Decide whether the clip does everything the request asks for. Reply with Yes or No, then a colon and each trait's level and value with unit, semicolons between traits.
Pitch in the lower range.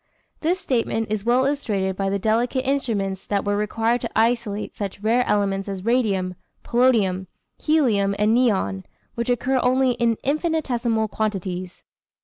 No: high, 225 Hz